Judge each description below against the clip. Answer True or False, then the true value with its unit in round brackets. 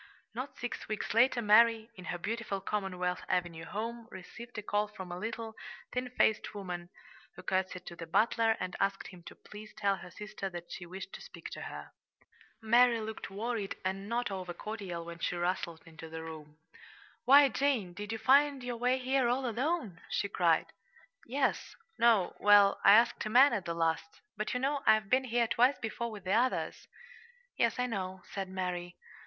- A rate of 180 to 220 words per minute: True (185 wpm)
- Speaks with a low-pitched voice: False (210 Hz)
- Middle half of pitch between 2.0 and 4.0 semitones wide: False (4.5 semitones)